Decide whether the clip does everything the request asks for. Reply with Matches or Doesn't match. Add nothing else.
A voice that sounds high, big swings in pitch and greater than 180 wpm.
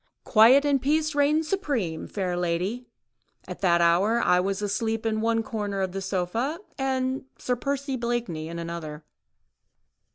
Doesn't match